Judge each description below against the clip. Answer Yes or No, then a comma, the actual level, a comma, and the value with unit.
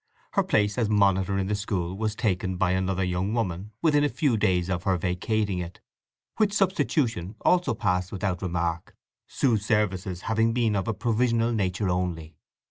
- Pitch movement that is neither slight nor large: Yes, average, 3.7 semitones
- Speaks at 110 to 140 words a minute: No, average, 170 wpm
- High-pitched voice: No, low, 100 Hz